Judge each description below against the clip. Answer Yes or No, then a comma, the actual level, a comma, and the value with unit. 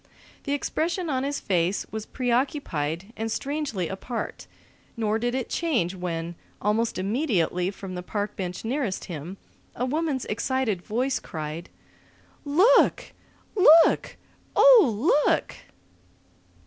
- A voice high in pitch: Yes, high, 225 Hz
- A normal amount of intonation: No, wide, 7.4 semitones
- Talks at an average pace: No, slow, 115 wpm